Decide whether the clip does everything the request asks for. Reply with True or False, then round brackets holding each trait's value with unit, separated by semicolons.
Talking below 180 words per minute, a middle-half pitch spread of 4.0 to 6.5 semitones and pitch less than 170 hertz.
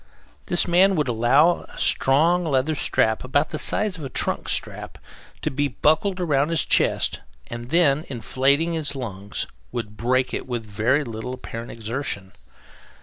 True (155 wpm; 5.1 semitones; 135 Hz)